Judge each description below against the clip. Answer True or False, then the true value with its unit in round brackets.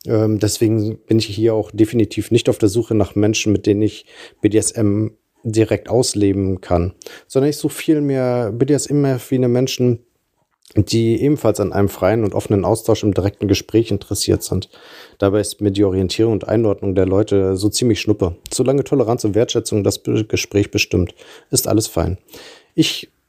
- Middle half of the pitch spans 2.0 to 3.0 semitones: True (2.4 semitones)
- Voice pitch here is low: True (110 Hz)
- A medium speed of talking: True (160 wpm)